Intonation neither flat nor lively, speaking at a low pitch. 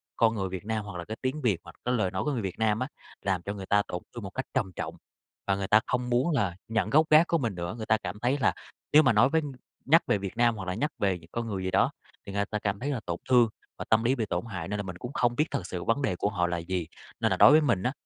Yes: average, 4.8 semitones; low, 110 Hz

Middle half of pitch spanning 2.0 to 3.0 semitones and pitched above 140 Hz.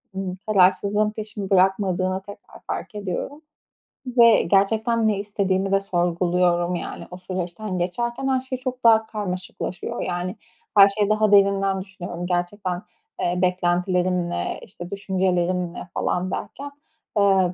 Yes: average, 2.7 semitones; high, 190 Hz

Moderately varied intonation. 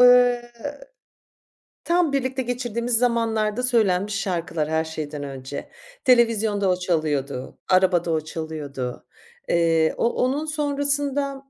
No: wide, 7.7 semitones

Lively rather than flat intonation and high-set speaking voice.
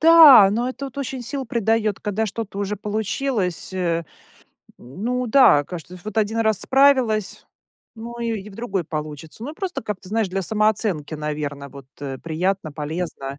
Yes: wide, 5.9 semitones; high, 210 Hz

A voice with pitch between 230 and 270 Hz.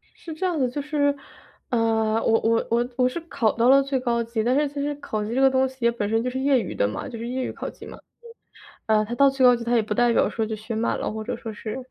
Yes: high, 240 Hz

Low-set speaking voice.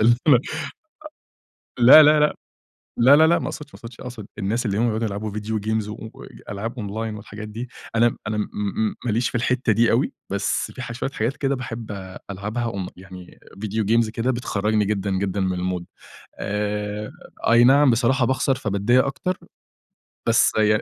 Yes: low, 110 Hz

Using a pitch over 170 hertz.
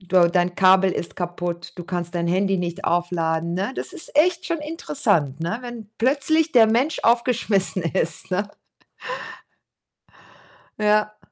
Yes: high, 190 Hz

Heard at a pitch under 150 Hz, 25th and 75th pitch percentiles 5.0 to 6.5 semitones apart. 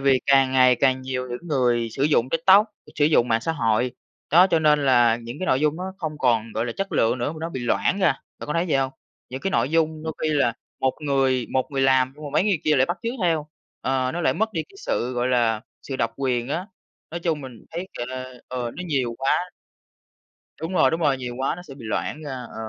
No: low, 135 Hz; average, 4.2 semitones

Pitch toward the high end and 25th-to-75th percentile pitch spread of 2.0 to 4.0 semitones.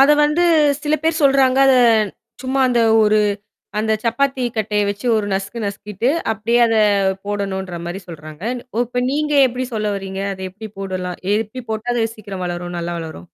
No: high, 215 Hz; average, 4.5 semitones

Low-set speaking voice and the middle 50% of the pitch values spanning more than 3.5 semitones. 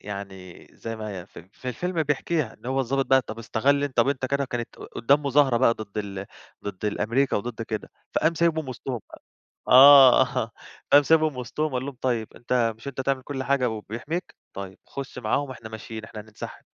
Yes: low, 125 Hz; average, 4.0 semitones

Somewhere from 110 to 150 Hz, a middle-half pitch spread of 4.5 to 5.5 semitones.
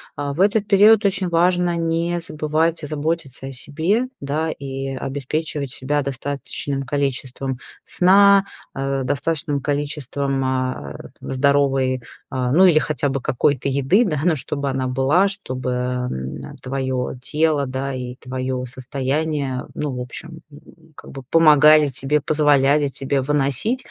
No: medium, 140 Hz; average, 3.3 semitones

